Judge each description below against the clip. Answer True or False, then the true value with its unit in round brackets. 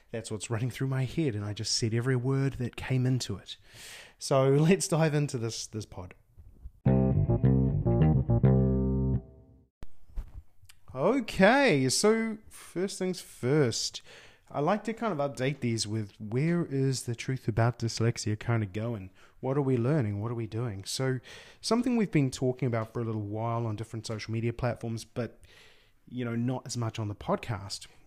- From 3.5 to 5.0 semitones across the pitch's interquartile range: True (4.0 semitones)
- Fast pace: False (165 wpm)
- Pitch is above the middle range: False (120 Hz)